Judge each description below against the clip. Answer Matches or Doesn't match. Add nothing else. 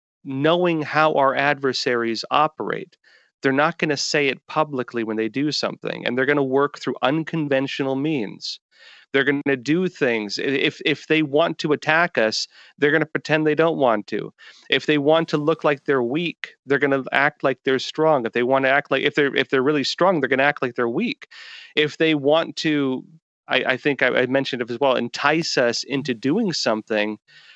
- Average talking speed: Doesn't match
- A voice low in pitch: Doesn't match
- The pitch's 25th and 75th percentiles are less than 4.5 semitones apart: Matches